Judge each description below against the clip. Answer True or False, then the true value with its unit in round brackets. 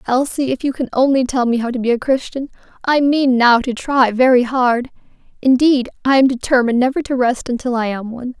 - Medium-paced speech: False (215 wpm)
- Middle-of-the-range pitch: False (255 Hz)